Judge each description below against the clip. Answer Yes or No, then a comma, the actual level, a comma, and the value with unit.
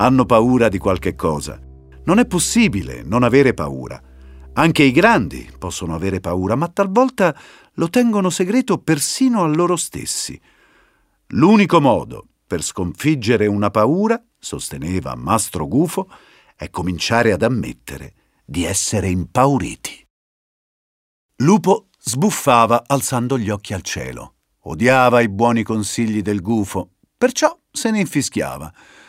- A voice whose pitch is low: Yes, low, 120 Hz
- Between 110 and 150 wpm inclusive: Yes, average, 120 wpm